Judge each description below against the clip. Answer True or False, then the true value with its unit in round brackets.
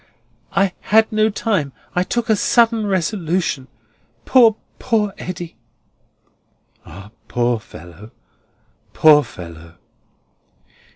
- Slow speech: True (95 wpm)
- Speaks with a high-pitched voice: False (180 Hz)